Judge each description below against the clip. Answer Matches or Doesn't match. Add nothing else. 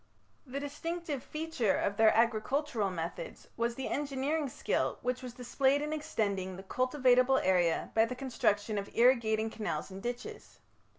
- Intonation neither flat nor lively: Matches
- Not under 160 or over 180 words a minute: Doesn't match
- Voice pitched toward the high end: Matches